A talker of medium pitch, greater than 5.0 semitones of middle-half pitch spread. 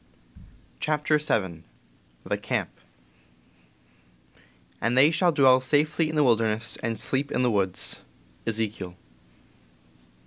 No: low, 125 Hz; wide, 5.5 semitones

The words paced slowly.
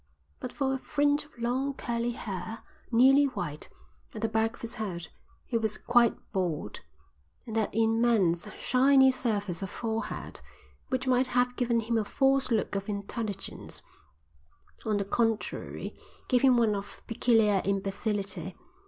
No: average, 145 wpm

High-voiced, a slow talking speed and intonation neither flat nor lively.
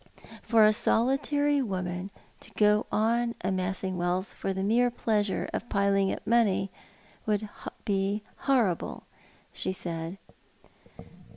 Yes: high, 205 Hz; slow, 120 wpm; average, 3.5 semitones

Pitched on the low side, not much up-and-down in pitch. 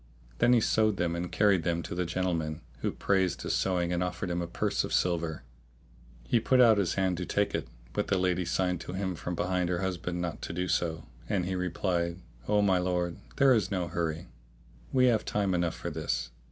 Yes: very low, 90 Hz; narrow, 1.9 semitones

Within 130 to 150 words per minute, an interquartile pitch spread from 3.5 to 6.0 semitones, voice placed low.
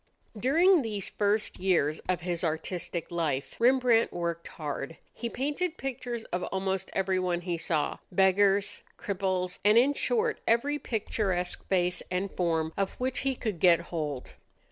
No: average, 145 wpm; wide, 5.4 semitones; high, 190 Hz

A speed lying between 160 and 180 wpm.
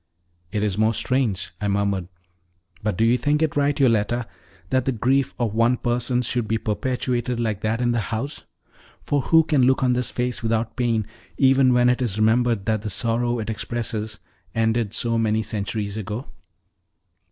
Yes: average, 175 wpm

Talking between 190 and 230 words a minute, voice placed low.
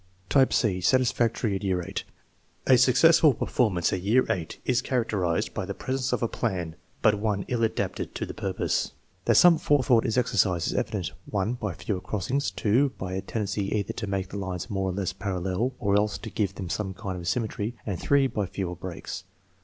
Yes: average, 200 wpm; low, 105 Hz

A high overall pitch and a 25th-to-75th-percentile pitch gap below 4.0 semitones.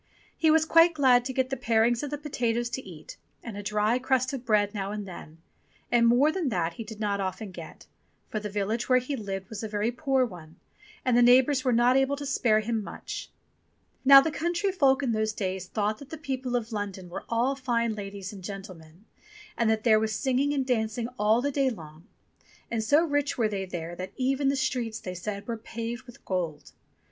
No: high, 230 Hz; average, 4.3 semitones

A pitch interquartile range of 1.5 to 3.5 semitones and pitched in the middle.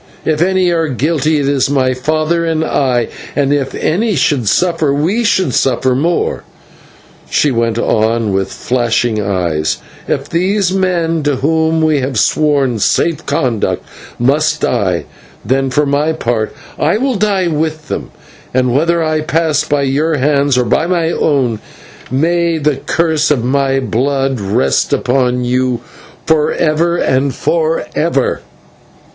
No: average, 4.2 semitones; medium, 145 Hz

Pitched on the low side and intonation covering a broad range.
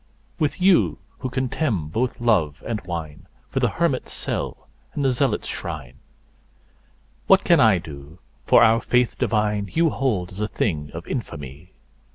Yes: low, 105 Hz; wide, 8.4 semitones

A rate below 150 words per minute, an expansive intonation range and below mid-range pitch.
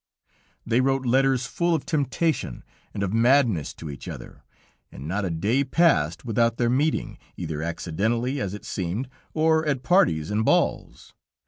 No: average, 155 wpm; wide, 6.7 semitones; low, 120 Hz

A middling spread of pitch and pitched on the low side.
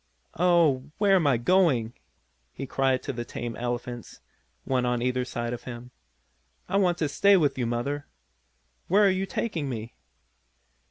No: wide, 6.3 semitones; low, 130 Hz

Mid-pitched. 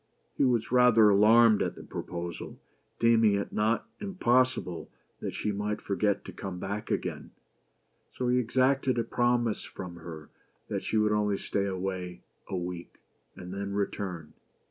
No: low, 105 Hz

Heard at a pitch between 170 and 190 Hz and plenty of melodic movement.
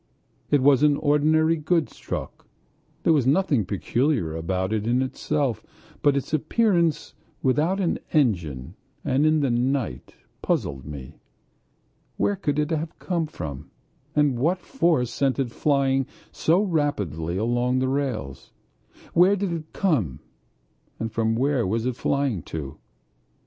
No: low, 135 Hz; wide, 5.7 semitones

